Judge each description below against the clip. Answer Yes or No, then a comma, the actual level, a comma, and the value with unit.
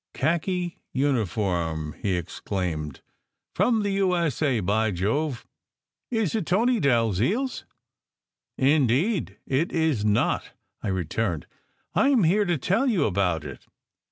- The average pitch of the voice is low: Yes, low, 130 Hz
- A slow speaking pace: Yes, slow, 130 wpm